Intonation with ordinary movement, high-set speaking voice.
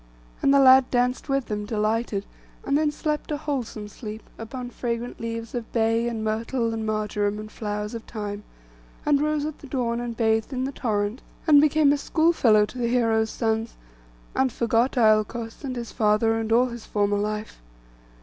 Yes: average, 3.2 semitones; high, 230 Hz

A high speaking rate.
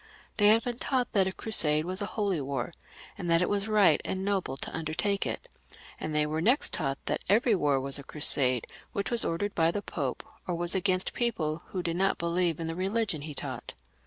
Yes: fast, 220 wpm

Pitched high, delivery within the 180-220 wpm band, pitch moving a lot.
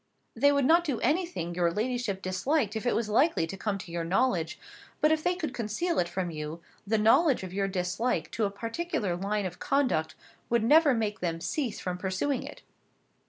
Yes: high, 215 Hz; average, 200 wpm; wide, 7.1 semitones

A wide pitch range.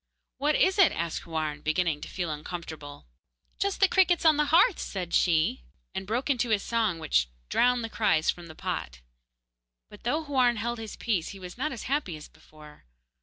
Yes: wide, 8.8 semitones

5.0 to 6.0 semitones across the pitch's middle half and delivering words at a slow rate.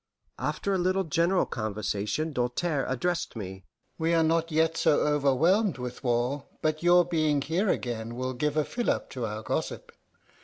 No: wide, 5.5 semitones; average, 160 wpm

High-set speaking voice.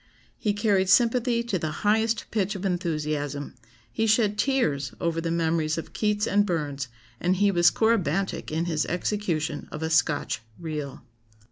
No: medium, 175 Hz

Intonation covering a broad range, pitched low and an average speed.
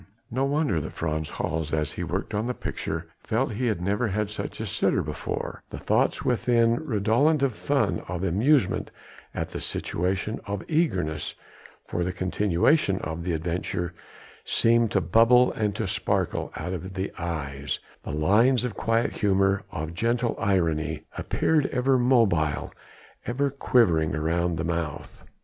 Yes: wide, 6.0 semitones; low, 100 Hz; average, 155 wpm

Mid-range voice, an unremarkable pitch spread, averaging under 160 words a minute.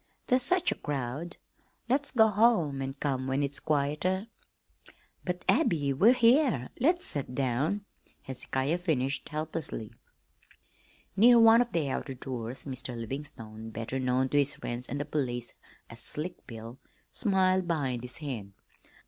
No: medium, 145 Hz; wide, 6.5 semitones; average, 140 wpm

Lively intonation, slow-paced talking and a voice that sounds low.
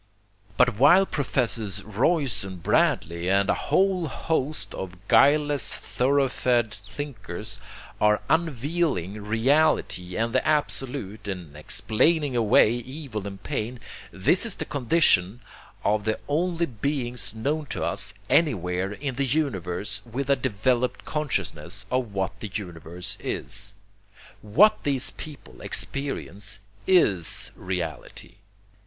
Yes: wide, 6.5 semitones; slow, 115 wpm; low, 115 Hz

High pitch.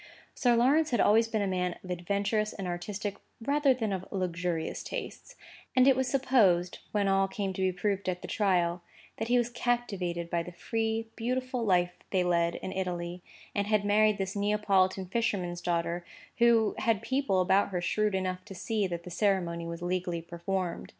Yes: high, 195 Hz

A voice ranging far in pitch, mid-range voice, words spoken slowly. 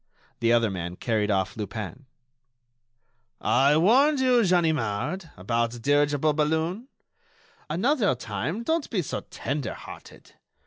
Yes: wide, 8.5 semitones; medium, 145 Hz; slow, 120 wpm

